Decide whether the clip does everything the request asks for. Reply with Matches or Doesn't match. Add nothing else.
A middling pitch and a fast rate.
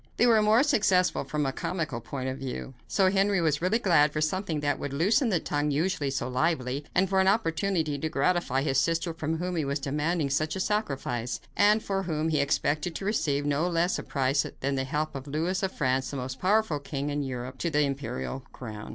Matches